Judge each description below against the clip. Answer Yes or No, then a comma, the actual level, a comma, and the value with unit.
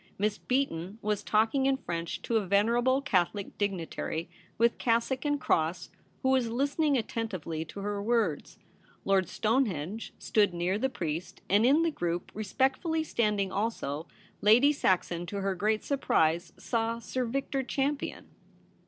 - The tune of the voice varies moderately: No, wide, 5.8 semitones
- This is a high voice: Yes, high, 215 Hz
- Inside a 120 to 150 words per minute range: Yes, average, 145 wpm